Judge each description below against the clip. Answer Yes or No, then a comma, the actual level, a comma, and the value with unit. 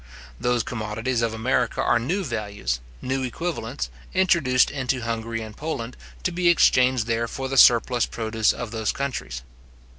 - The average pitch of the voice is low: Yes, low, 120 Hz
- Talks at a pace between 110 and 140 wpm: No, average, 150 wpm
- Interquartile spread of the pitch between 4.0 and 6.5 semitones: No, average, 3.0 semitones